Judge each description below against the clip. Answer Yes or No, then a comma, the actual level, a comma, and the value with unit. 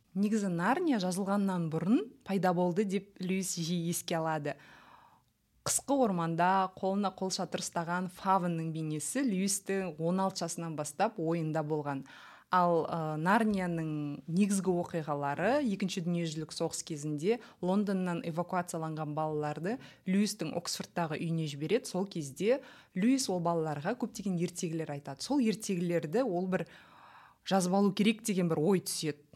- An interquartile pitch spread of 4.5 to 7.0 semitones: No, average, 3.4 semitones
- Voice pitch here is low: No, medium, 180 Hz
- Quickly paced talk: No, average, 120 wpm